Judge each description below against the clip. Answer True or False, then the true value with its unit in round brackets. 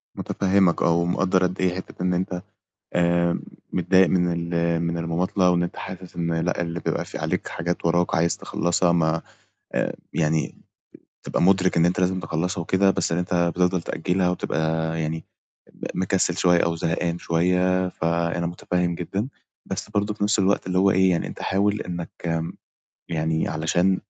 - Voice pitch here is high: False (90 Hz)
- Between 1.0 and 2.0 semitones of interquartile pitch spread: True (1.7 semitones)